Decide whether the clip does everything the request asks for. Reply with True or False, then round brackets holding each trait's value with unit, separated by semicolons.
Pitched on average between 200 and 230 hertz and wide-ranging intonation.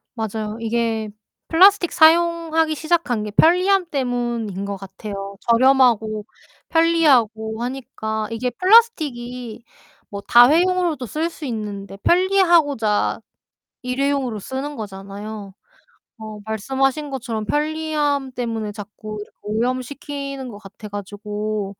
False (245 Hz; 5.8 semitones)